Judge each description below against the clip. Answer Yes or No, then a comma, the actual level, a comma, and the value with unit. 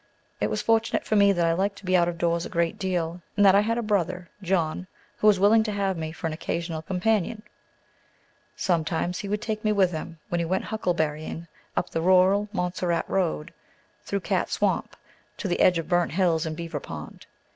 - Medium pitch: Yes, medium, 180 Hz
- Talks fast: Yes, fast, 210 wpm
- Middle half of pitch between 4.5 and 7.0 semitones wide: No, average, 3.1 semitones